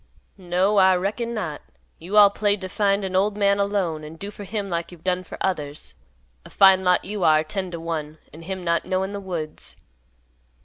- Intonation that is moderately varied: Yes, average, 3.1 semitones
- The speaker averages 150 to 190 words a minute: No, fast, 205 wpm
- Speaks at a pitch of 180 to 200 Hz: Yes, medium, 185 Hz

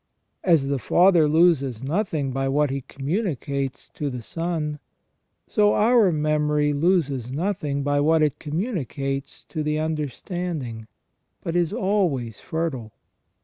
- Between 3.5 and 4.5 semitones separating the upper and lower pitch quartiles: Yes, average, 3.9 semitones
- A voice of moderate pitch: Yes, medium, 150 Hz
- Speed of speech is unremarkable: No, slow, 125 wpm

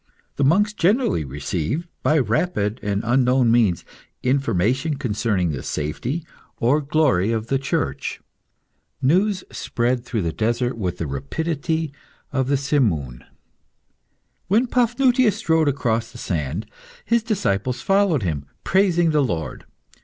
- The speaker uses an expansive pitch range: Yes, wide, 7.9 semitones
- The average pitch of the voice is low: Yes, low, 130 Hz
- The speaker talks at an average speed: No, slow, 125 wpm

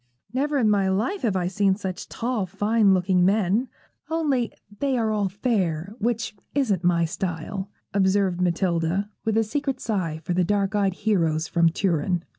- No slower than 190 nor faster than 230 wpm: No, average, 165 wpm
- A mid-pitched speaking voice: No, high, 195 Hz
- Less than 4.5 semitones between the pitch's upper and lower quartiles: Yes, average, 3.6 semitones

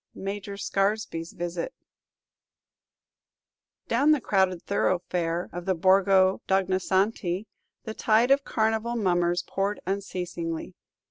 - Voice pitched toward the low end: No, high, 190 Hz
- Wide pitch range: No, average, 2.9 semitones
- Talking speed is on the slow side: Yes, slow, 105 wpm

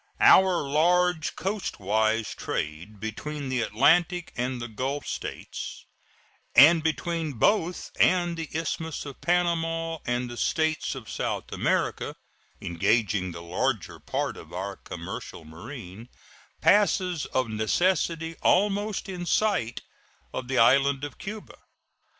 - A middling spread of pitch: No, wide, 7.3 semitones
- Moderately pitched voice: Yes, medium, 145 Hz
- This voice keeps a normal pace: No, slow, 120 wpm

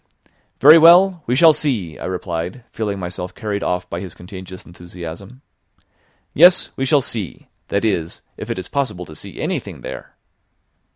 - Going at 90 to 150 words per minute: No, average, 160 wpm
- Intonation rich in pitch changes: Yes, wide, 7.0 semitones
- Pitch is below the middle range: Yes, low, 100 Hz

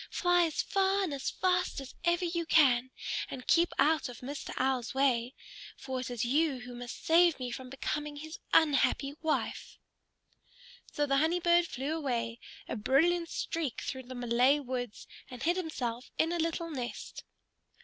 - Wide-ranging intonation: No, average, 4.8 semitones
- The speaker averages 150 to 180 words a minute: Yes, average, 170 wpm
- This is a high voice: Yes, very high, 280 Hz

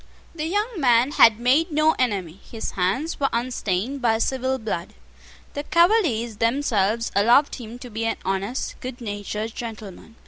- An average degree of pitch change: Yes, average, 4.5 semitones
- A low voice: No, high, 235 Hz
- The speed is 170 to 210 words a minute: No, average, 150 wpm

